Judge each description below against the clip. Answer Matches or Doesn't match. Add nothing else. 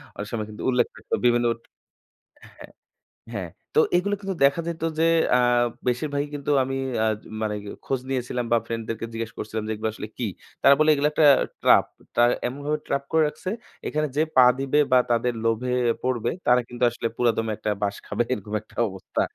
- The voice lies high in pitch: Doesn't match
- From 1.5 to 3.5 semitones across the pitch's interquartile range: Doesn't match